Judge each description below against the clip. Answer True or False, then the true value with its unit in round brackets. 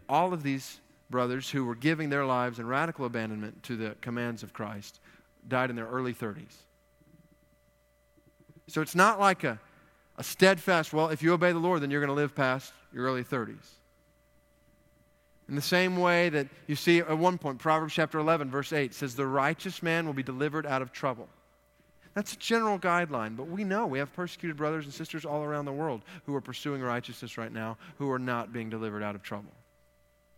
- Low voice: False (145 Hz)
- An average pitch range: True (4.9 semitones)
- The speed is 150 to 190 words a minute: False (200 wpm)